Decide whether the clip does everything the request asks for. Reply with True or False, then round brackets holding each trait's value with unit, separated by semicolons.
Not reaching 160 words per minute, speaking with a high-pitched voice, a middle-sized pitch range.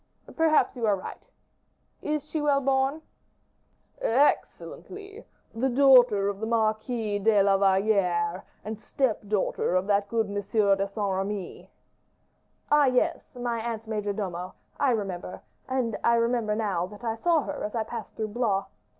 True (150 wpm; 220 Hz; 3.9 semitones)